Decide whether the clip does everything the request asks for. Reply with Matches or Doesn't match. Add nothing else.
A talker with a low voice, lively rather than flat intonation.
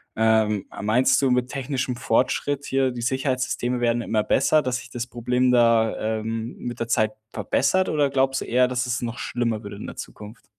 Doesn't match